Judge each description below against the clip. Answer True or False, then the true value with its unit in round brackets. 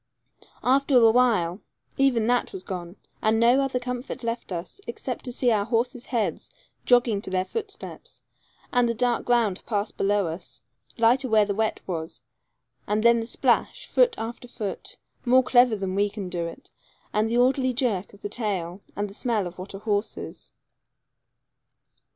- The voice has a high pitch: True (225 Hz)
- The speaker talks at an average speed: True (170 wpm)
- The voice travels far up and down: False (3.7 semitones)